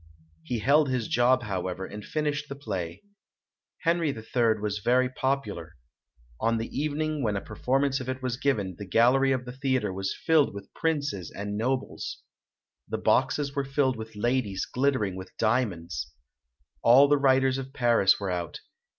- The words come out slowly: No, average, 160 wpm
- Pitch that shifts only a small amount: No, average, 4.9 semitones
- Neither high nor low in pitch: No, low, 125 Hz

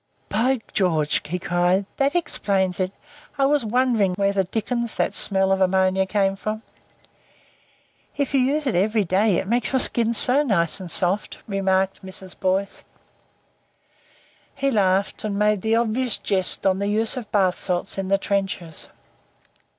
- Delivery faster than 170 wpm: No, average, 160 wpm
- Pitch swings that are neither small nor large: Yes, average, 3.3 semitones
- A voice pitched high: Yes, high, 200 Hz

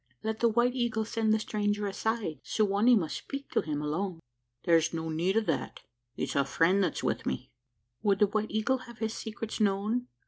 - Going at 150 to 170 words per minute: No, fast, 205 wpm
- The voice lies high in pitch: Yes, high, 210 Hz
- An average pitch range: Yes, average, 4.3 semitones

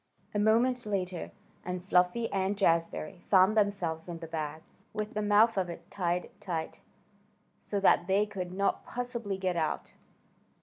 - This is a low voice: No, high, 190 Hz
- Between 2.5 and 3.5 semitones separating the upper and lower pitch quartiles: Yes, average, 3.1 semitones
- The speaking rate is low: No, average, 150 wpm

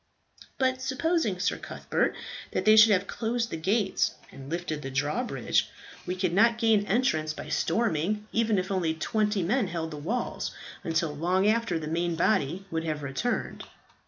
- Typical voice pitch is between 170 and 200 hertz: Yes, high, 190 Hz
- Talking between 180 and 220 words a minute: No, average, 165 wpm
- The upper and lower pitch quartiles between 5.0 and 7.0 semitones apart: Yes, wide, 5.6 semitones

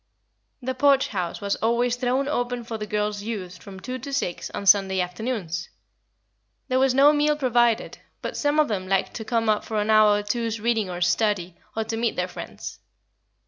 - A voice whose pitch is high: Yes, high, 220 Hz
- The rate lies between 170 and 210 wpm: Yes, average, 195 wpm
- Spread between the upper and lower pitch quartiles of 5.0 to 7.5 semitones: No, average, 3.7 semitones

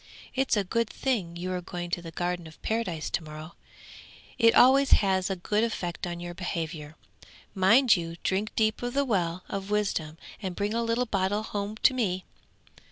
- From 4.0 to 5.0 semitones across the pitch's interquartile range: Yes, average, 4.3 semitones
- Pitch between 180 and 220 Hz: Yes, high, 190 Hz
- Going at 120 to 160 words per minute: No, average, 185 wpm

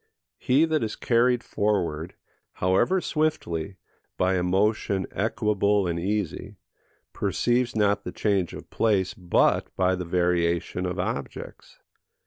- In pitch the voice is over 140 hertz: No, low, 100 Hz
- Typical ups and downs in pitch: Yes, average, 3.5 semitones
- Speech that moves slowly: Yes, slow, 120 wpm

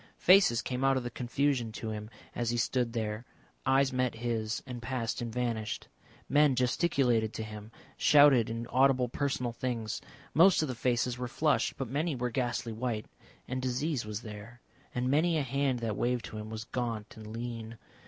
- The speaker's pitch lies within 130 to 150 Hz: No, low, 120 Hz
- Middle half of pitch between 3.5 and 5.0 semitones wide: No, average, 2.7 semitones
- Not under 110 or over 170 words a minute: No, average, 180 wpm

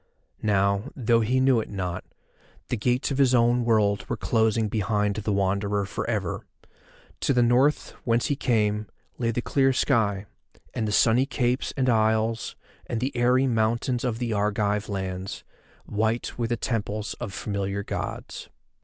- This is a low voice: Yes, low, 110 Hz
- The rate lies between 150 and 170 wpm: Yes, average, 160 wpm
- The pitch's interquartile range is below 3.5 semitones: Yes, average, 3.0 semitones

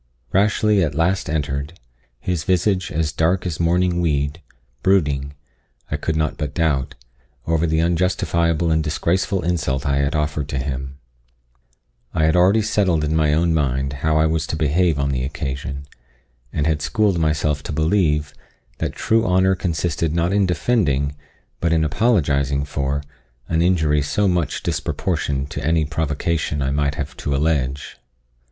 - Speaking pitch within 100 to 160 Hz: No, very low, 80 Hz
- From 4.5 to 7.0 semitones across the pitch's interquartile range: No, average, 3.4 semitones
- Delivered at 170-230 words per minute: No, average, 155 wpm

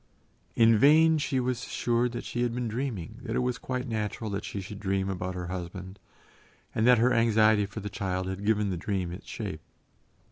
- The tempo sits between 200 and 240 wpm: Yes, fast, 205 wpm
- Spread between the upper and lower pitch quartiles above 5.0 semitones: No, average, 4.1 semitones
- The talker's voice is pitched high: No, low, 110 Hz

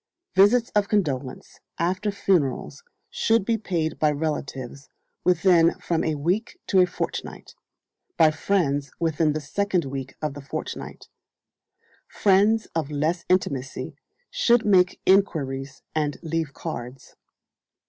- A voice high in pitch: No, medium, 165 Hz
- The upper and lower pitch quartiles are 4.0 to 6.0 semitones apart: Yes, average, 5.1 semitones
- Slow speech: Yes, slow, 120 wpm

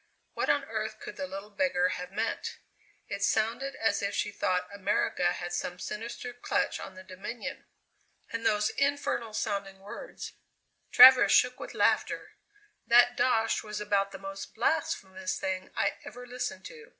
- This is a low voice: No, high, 210 Hz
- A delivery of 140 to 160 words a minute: Yes, average, 155 wpm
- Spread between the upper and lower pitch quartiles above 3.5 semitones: Yes, average, 4.2 semitones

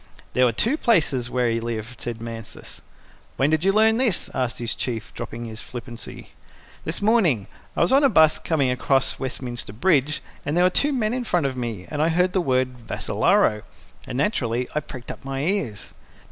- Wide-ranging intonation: Yes, wide, 7.2 semitones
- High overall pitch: No, low, 135 Hz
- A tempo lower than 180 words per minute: No, average, 195 wpm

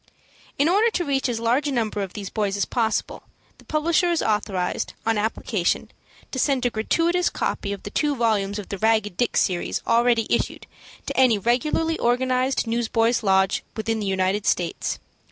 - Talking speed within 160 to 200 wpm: Yes, average, 175 wpm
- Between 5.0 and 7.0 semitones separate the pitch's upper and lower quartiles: No, average, 4.4 semitones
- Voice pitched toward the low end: No, high, 230 Hz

